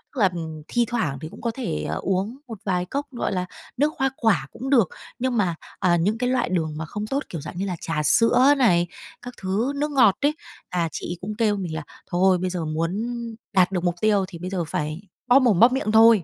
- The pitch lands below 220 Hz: Yes, high, 195 Hz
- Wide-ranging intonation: Yes, wide, 5.7 semitones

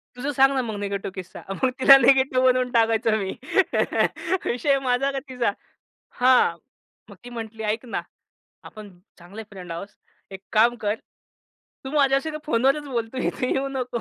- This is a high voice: Yes, high, 245 Hz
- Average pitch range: Yes, average, 3.5 semitones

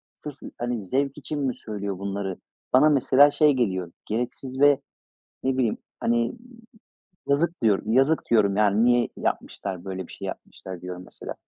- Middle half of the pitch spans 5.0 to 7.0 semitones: Yes, wide, 5.5 semitones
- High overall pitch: No, low, 120 Hz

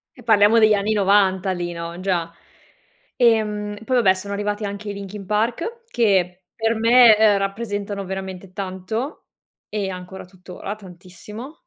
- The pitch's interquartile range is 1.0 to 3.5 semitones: Yes, narrow, 2.5 semitones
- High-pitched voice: Yes, high, 200 Hz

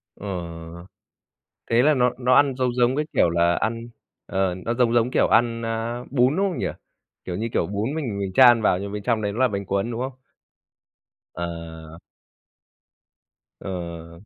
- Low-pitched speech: Yes, low, 115 Hz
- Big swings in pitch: No, average, 4.6 semitones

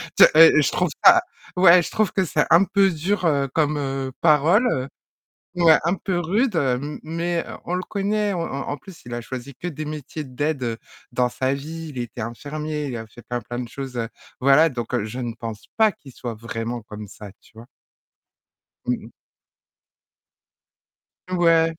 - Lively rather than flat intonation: Yes, wide, 5.7 semitones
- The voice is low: No, medium, 150 Hz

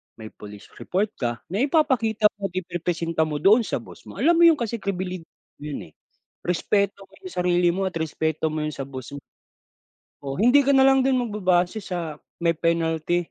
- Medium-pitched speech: Yes, medium, 180 Hz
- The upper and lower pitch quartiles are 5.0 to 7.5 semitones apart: Yes, average, 5.3 semitones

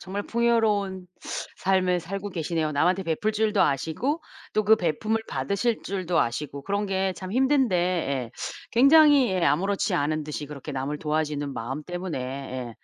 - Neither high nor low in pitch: Yes, medium, 180 Hz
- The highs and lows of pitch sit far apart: Yes, wide, 5.7 semitones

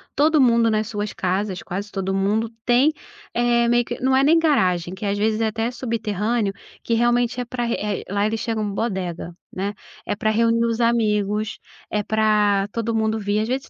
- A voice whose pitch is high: Yes, high, 220 Hz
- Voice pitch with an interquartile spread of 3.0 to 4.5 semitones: No, narrow, 2.6 semitones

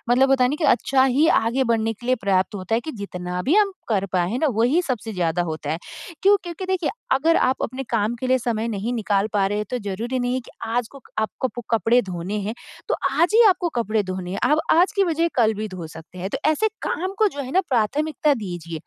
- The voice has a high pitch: Yes, high, 235 Hz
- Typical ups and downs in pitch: No, wide, 6.1 semitones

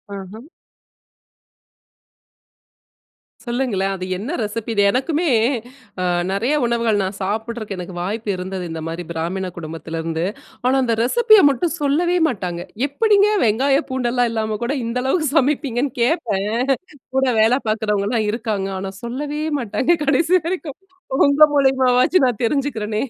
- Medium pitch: No, high, 235 Hz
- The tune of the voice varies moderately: No, wide, 5.7 semitones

